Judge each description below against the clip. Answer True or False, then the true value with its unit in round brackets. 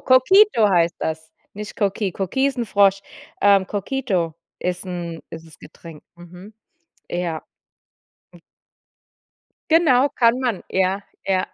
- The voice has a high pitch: True (195 Hz)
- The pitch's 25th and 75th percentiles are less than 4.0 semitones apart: False (5.2 semitones)